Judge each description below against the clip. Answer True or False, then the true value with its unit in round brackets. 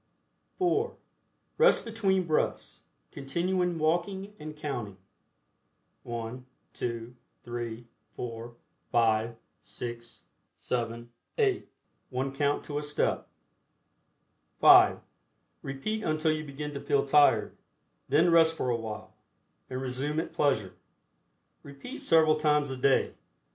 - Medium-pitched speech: True (145 Hz)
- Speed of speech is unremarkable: False (110 wpm)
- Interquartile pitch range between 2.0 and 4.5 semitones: False (5.2 semitones)